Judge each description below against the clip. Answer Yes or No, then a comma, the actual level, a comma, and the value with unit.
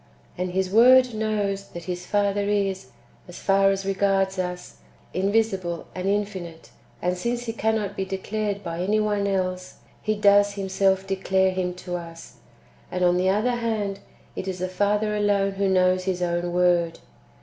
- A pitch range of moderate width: No, narrow, 2.1 semitones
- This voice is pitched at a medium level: No, high, 195 Hz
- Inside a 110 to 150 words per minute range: No, average, 170 wpm